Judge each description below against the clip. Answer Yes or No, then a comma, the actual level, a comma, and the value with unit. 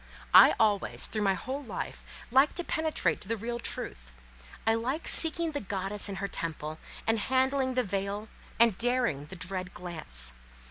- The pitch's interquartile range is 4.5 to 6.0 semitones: Yes, wide, 5.6 semitones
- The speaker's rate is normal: Yes, average, 170 wpm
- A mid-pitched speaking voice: No, high, 215 Hz